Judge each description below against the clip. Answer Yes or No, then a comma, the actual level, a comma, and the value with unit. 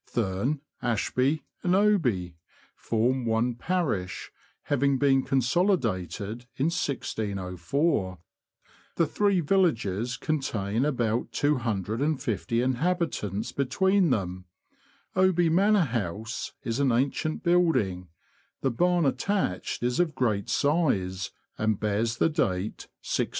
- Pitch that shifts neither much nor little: No, wide, 7.1 semitones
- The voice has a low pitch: Yes, low, 125 Hz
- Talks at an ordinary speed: No, slow, 105 wpm